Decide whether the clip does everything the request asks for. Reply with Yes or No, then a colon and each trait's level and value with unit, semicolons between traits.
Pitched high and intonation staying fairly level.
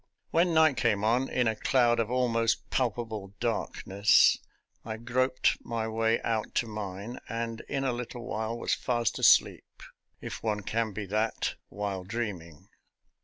No: low, 115 Hz; narrow, 2.2 semitones